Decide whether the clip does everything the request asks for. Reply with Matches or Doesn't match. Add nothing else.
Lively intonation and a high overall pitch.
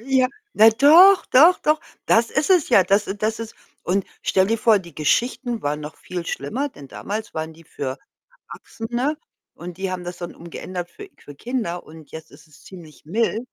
Matches